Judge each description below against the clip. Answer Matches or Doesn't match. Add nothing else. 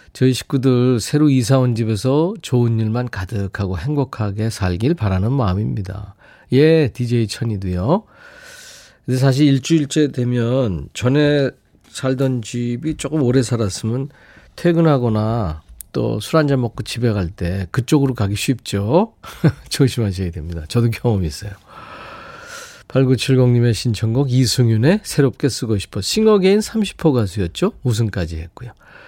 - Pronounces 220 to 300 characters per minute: Matches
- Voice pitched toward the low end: Matches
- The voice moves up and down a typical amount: Matches